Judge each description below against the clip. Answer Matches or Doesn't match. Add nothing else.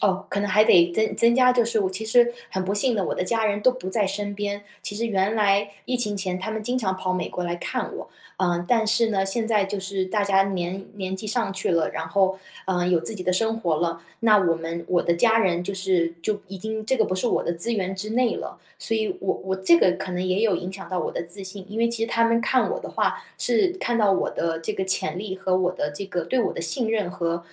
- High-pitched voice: Matches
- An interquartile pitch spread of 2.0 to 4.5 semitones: Matches